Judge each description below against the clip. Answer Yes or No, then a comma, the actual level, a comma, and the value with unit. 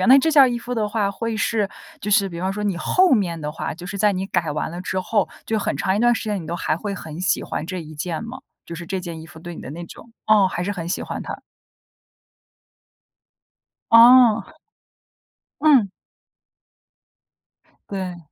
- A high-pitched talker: Yes, high, 195 Hz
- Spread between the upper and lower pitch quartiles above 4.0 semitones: Yes, average, 4.5 semitones